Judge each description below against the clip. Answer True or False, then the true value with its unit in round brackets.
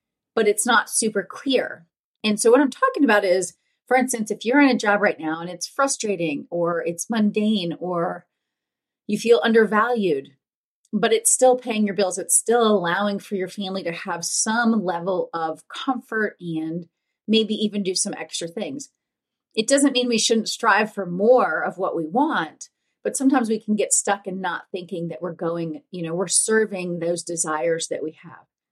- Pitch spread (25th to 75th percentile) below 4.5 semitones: False (5.1 semitones)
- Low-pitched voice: False (210 Hz)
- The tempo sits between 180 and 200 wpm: True (185 wpm)